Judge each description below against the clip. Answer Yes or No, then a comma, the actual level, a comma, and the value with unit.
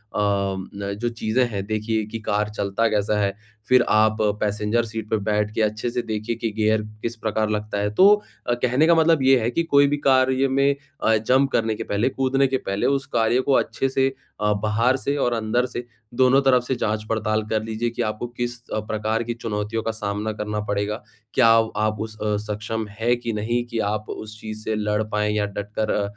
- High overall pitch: No, low, 110 Hz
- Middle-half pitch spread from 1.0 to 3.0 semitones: Yes, narrow, 2.5 semitones